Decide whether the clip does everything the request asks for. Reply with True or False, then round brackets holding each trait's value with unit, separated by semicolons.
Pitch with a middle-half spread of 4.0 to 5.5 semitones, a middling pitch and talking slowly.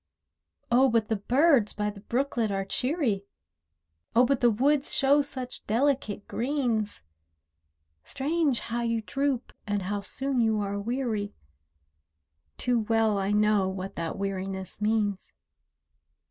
False (4.4 semitones; 225 Hz; 130 wpm)